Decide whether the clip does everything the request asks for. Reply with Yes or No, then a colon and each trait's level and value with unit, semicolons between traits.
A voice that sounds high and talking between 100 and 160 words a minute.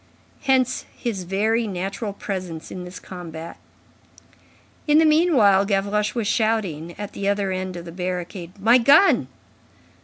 Yes: high, 200 Hz; average, 140 wpm